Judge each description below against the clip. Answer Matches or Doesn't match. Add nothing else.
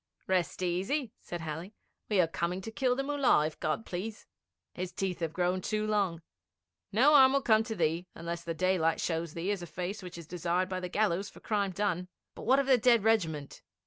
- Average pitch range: Matches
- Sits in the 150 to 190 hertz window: Matches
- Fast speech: Matches